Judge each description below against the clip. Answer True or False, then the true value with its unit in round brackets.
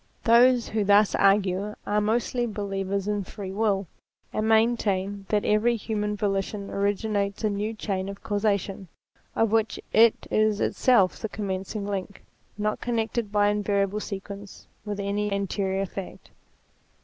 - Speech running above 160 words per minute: False (140 wpm)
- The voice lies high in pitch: True (205 Hz)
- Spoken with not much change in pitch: True (1.4 semitones)